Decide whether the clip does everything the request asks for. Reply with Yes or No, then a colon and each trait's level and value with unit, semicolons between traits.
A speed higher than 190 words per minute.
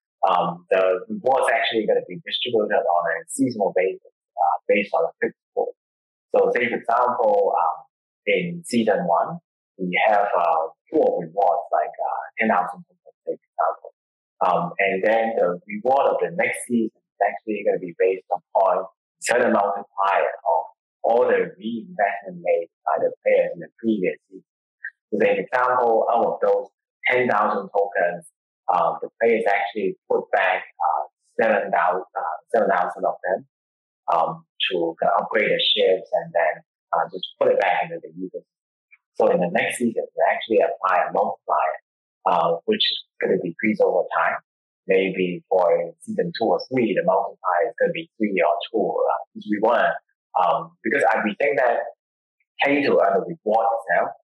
No: average, 170 wpm